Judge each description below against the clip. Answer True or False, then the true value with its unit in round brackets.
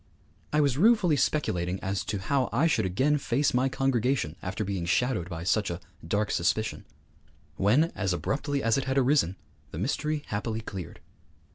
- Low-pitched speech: True (115 Hz)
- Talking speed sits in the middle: True (165 wpm)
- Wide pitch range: True (6.7 semitones)